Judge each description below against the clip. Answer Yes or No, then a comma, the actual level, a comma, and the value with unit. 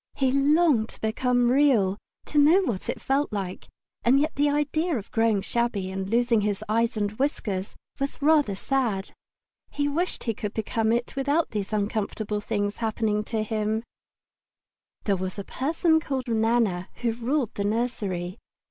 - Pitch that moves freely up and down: No, average, 4.9 semitones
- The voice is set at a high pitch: Yes, high, 230 Hz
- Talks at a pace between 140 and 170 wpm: Yes, average, 165 wpm